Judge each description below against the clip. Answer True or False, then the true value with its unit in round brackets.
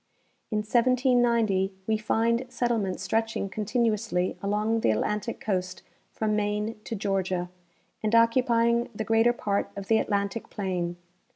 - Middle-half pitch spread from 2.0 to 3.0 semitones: True (2.7 semitones)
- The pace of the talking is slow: True (125 wpm)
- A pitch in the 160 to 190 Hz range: False (215 Hz)